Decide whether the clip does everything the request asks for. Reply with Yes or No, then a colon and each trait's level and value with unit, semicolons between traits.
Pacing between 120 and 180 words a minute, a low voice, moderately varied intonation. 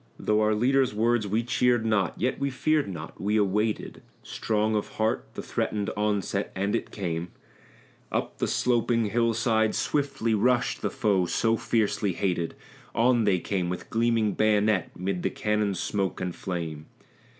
Yes: average, 160 wpm; low, 105 Hz; average, 3.0 semitones